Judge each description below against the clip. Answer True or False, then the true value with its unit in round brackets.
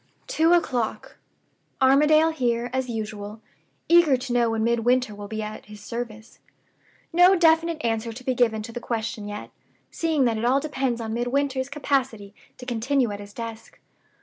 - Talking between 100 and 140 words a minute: False (165 wpm)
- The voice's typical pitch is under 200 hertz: False (240 Hz)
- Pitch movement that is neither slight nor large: True (3.8 semitones)